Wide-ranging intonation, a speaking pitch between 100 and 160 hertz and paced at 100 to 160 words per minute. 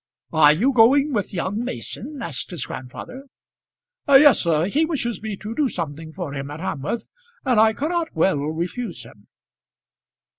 No: wide, 8.5 semitones; high, 205 Hz; average, 155 wpm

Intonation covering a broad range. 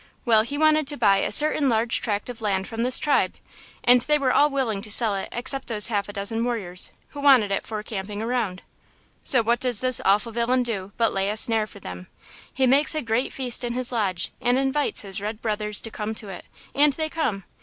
No: average, 3.8 semitones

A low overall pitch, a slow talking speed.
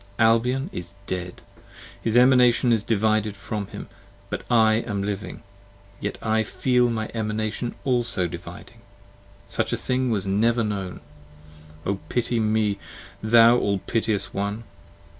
Yes: low, 110 Hz; slow, 125 wpm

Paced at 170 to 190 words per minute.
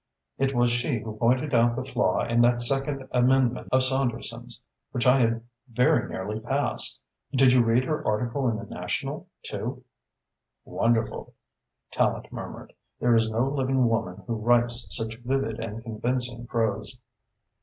No: average, 150 wpm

